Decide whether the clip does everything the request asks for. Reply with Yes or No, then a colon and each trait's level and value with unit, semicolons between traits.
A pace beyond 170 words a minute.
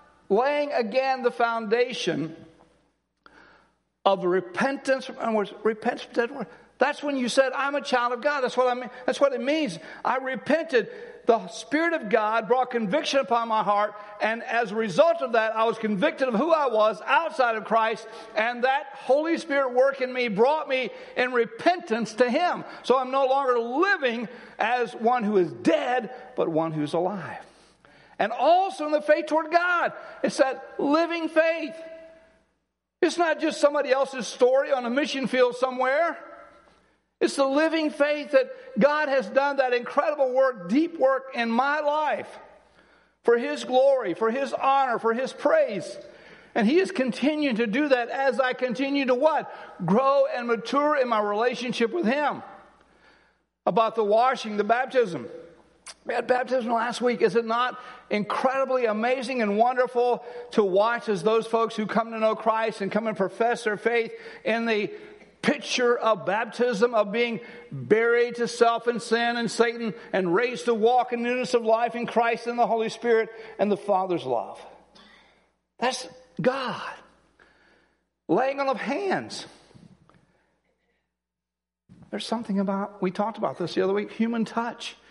No: average, 160 wpm